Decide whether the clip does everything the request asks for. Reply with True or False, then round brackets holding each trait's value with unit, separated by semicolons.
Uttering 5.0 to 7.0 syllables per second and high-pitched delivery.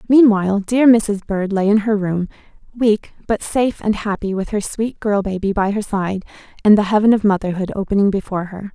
True (5.5 syllables/s; 205 Hz)